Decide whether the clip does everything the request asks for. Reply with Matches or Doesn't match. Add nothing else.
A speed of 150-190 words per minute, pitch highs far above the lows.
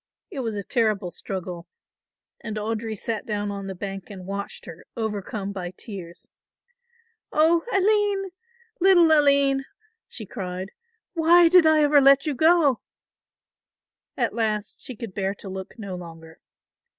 Doesn't match